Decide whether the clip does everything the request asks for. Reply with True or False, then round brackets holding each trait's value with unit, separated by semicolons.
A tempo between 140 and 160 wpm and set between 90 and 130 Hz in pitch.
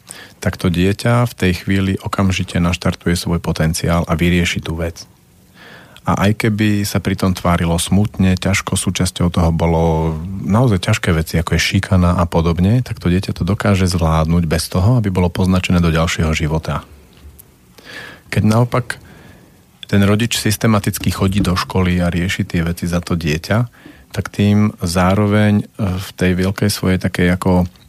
True (150 wpm; 95 Hz)